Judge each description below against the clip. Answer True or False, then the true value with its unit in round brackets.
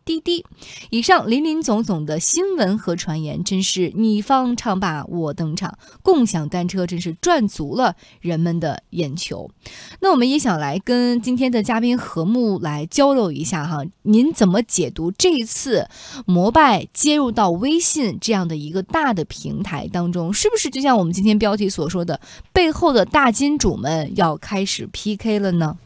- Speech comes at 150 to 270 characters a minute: True (260 characters per minute)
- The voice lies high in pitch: True (205 Hz)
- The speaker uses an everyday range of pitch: False (6.5 semitones)